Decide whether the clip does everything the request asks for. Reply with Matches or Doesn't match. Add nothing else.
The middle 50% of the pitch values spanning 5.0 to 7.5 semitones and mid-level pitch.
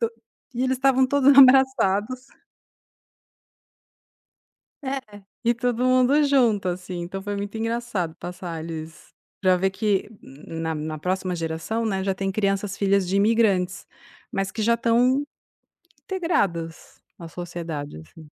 Doesn't match